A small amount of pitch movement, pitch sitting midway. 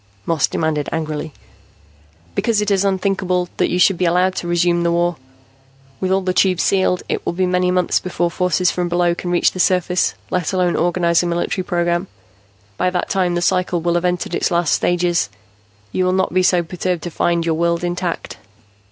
Yes: narrow, 1.1 semitones; medium, 175 Hz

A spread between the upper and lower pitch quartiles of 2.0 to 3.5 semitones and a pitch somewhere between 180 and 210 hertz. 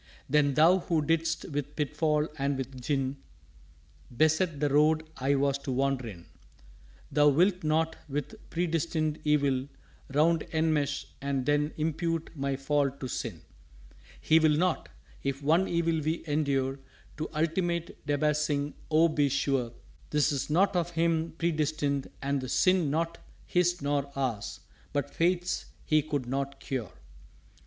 No: average, 2.7 semitones; medium, 150 Hz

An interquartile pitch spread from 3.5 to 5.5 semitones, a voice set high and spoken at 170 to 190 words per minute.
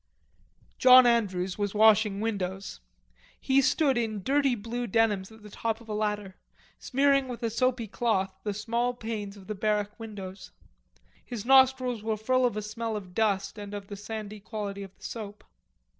No: average, 2.8 semitones; high, 215 Hz; average, 175 wpm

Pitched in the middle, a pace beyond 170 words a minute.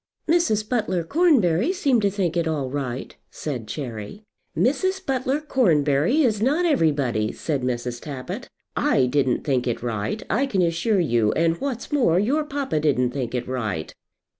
No: medium, 165 Hz; average, 160 wpm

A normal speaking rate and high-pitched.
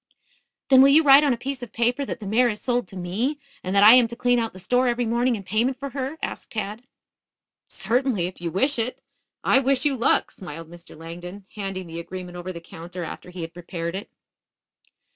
No: fast, 220 wpm; high, 220 Hz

